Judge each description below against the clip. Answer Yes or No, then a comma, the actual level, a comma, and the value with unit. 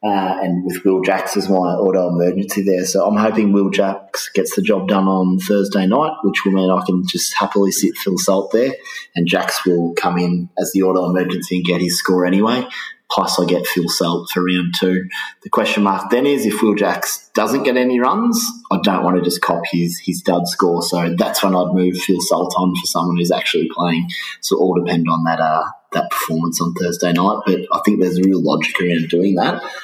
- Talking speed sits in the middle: No, fast, 225 wpm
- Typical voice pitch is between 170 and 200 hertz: No, very low, 90 Hz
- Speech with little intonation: Yes, narrow, 1.6 semitones